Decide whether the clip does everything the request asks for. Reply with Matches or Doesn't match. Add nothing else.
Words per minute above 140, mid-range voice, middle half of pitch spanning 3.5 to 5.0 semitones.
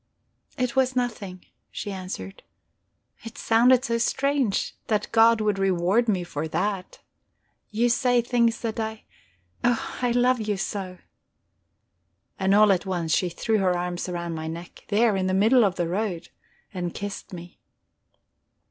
Doesn't match